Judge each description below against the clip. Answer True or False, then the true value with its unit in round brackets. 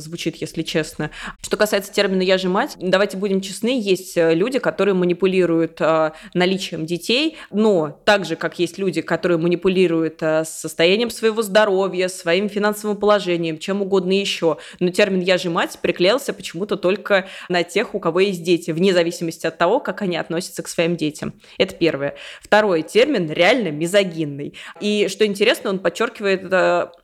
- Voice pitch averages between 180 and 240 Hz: True (185 Hz)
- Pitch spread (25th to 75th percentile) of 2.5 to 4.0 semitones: True (3.2 semitones)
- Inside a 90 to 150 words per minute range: False (160 wpm)